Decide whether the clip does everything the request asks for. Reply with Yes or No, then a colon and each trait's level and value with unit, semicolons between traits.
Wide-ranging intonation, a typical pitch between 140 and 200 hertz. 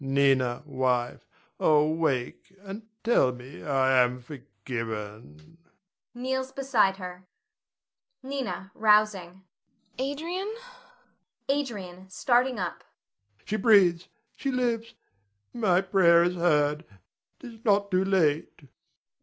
Yes: wide, 8.2 semitones; medium, 185 Hz